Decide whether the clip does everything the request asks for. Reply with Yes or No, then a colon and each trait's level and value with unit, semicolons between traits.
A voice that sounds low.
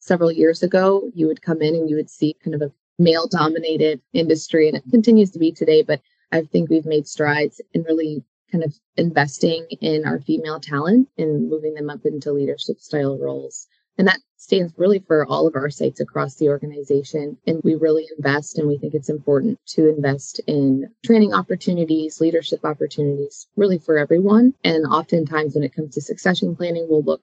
No: medium, 155 Hz